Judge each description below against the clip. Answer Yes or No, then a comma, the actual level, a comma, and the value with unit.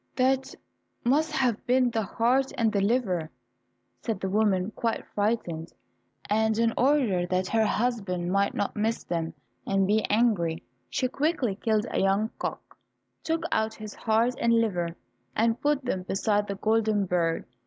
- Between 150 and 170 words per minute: Yes, average, 155 wpm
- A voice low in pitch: No, high, 220 Hz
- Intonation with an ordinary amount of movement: Yes, average, 3.6 semitones